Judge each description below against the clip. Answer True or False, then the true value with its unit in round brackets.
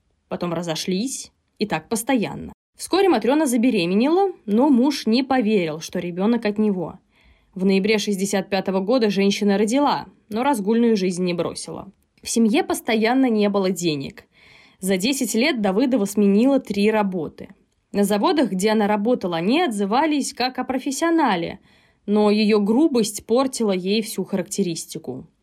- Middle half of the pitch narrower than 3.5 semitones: False (4.6 semitones)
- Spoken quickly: False (135 wpm)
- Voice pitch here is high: True (215 Hz)